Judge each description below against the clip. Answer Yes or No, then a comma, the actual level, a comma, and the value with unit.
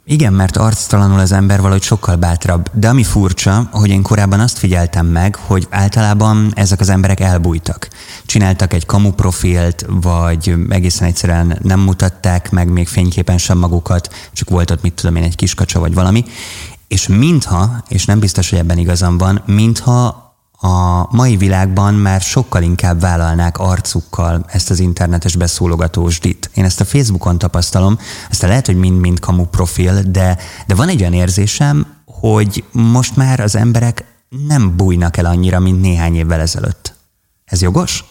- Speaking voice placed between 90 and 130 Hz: Yes, very low, 95 Hz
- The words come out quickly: Yes, fast, 160 wpm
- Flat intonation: No, average, 3.0 semitones